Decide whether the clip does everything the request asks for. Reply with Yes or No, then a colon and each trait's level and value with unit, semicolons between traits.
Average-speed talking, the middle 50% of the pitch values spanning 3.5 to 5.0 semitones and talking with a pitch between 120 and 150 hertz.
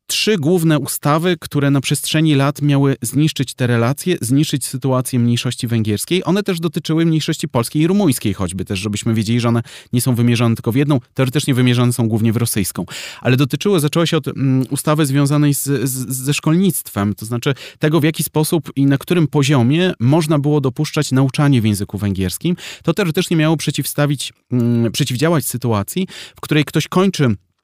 No: fast, 170 wpm; average, 4.5 semitones; medium, 140 Hz